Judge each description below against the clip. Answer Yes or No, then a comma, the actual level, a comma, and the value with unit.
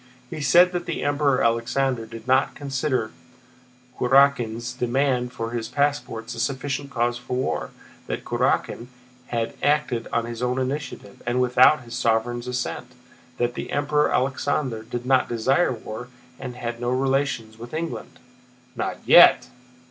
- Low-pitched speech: Yes, low, 125 Hz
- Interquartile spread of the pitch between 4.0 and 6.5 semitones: No, average, 2.8 semitones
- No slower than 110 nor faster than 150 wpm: Yes, average, 145 wpm